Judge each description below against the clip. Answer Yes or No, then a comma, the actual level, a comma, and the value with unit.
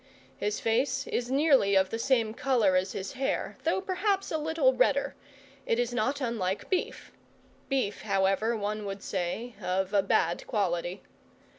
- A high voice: Yes, high, 225 Hz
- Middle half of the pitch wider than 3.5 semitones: Yes, wide, 5.6 semitones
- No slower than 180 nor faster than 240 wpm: No, average, 155 wpm